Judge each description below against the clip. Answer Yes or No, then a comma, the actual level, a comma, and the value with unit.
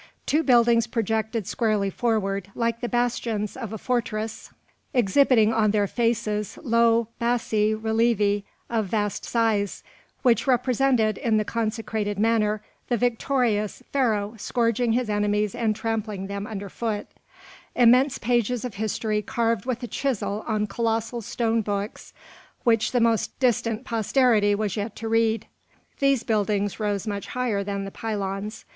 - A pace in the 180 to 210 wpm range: No, average, 140 wpm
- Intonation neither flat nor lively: No, narrow, 2.2 semitones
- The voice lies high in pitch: Yes, high, 225 Hz